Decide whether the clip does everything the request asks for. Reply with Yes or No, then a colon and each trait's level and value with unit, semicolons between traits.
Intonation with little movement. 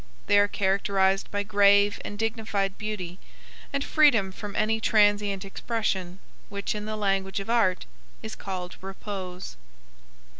Yes: narrow, 1.8 semitones